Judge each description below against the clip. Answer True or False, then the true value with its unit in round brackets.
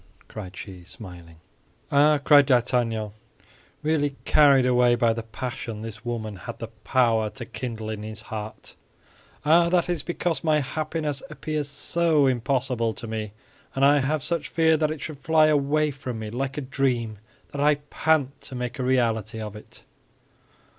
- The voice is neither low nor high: False (130 Hz)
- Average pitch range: True (4.8 semitones)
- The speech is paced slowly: False (165 wpm)